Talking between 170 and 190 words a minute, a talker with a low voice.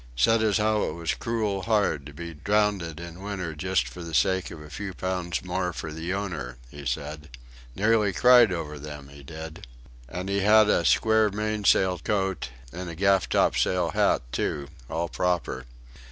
Yes: average, 175 wpm; very low, 90 Hz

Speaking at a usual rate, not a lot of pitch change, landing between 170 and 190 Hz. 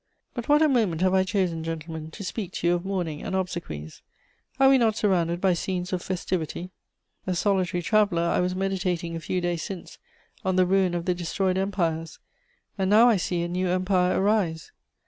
Yes: average, 195 wpm; narrow, 2.1 semitones; medium, 185 Hz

